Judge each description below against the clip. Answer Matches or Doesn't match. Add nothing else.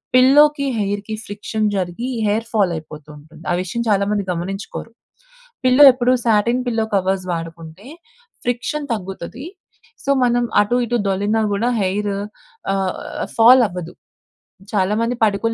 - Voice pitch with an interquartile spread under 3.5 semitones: Doesn't match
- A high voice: Matches